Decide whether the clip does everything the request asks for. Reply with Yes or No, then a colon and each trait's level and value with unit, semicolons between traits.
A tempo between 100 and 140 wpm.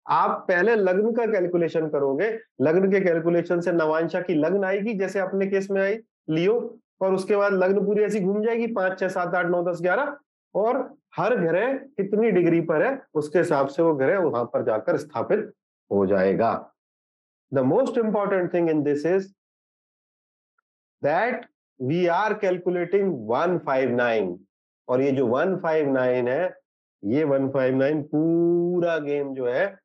No: average, 160 wpm